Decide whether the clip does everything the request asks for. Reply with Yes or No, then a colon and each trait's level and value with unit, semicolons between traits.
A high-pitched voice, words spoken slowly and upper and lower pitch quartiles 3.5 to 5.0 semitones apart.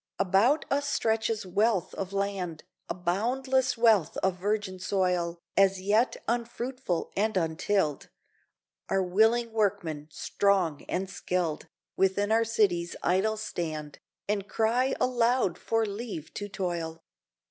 Yes: high, 200 Hz; slow, 120 wpm; average, 4.0 semitones